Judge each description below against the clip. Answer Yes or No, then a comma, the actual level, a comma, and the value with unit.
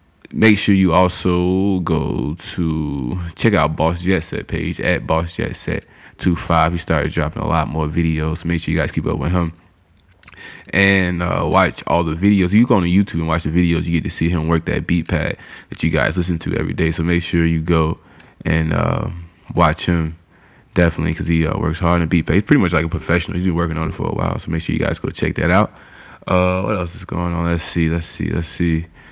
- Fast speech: Yes, fast, 240 wpm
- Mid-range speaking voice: No, very low, 85 Hz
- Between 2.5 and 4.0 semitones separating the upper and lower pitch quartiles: No, narrow, 2.1 semitones